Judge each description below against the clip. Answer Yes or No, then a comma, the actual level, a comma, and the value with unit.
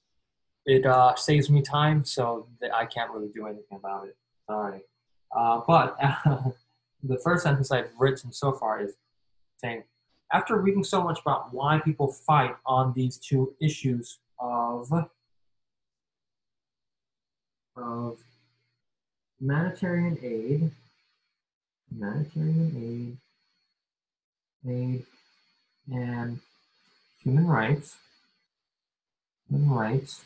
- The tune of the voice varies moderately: Yes, average, 3.6 semitones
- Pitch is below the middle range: Yes, low, 130 Hz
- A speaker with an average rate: No, slow, 105 wpm